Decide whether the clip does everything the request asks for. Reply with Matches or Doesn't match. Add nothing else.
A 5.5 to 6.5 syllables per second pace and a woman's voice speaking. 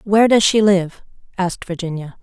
Matches